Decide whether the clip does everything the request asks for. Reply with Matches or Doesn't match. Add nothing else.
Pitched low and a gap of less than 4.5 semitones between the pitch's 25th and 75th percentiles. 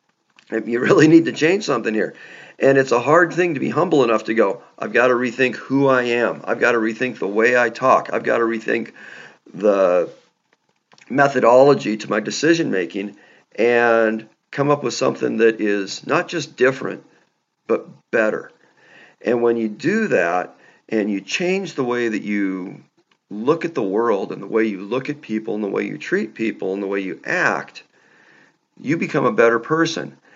Matches